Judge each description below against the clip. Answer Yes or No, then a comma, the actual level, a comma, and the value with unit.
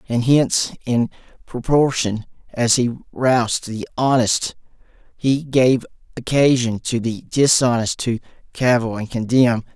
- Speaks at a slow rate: Yes, slow, 115 wpm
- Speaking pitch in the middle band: No, low, 120 Hz